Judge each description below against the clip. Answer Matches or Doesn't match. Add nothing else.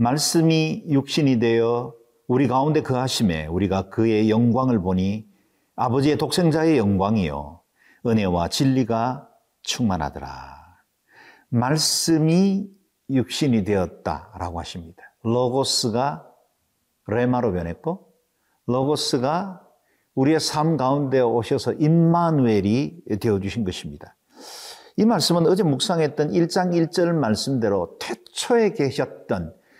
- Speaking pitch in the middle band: Doesn't match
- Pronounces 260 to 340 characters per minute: Doesn't match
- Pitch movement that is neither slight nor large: Doesn't match